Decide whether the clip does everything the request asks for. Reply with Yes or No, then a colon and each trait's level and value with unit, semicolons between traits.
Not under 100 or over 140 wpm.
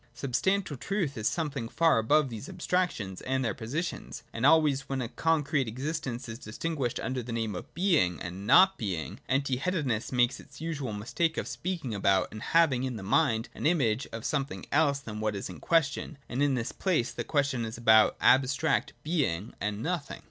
No: average, 200 wpm